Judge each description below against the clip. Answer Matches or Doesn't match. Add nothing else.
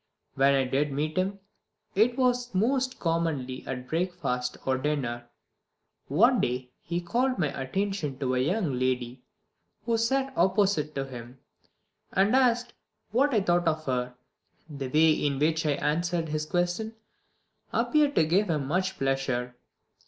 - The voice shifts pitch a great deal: Matches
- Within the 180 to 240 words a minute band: Doesn't match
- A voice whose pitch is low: Doesn't match